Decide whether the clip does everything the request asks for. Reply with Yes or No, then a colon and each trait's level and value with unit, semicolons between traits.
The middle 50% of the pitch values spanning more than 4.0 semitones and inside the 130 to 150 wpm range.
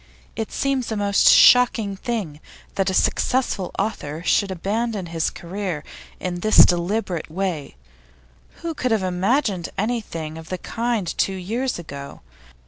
Yes: average, 4.6 semitones; slow, 135 wpm